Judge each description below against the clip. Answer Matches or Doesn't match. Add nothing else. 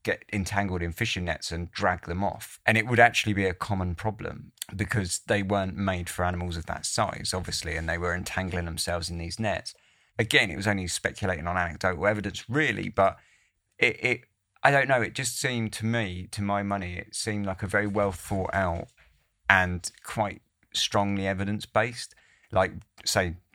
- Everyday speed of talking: Matches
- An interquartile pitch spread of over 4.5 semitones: Doesn't match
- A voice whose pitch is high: Doesn't match